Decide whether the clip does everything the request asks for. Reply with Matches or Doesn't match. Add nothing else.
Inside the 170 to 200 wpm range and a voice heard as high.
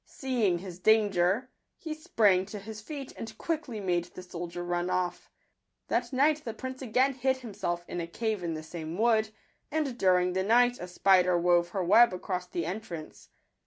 Matches